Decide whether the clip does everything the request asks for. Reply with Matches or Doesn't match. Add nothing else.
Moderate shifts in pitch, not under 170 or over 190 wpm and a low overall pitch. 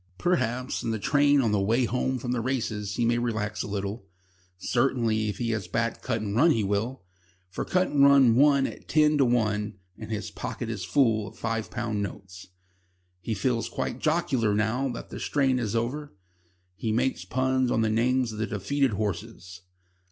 Matches